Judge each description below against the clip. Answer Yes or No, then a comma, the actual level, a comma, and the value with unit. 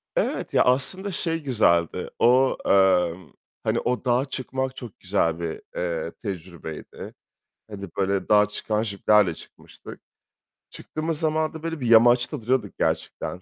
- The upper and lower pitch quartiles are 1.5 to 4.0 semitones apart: No, wide, 5.6 semitones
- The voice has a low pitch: Yes, low, 115 Hz